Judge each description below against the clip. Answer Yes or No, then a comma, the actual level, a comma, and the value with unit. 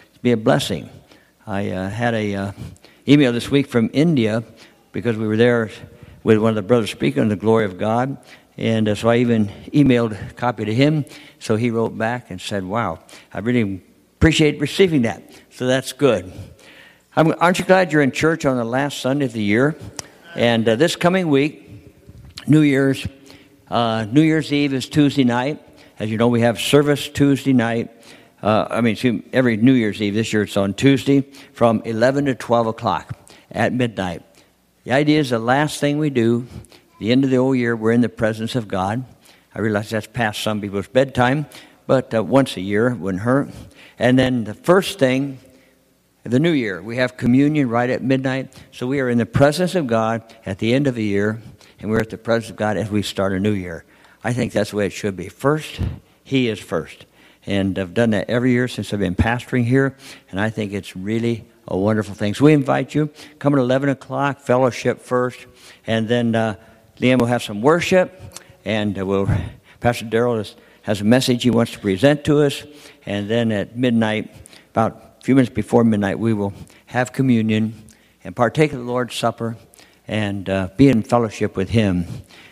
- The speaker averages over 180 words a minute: Yes, average, 200 wpm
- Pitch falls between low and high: No, low, 120 Hz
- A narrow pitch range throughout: No, average, 3.7 semitones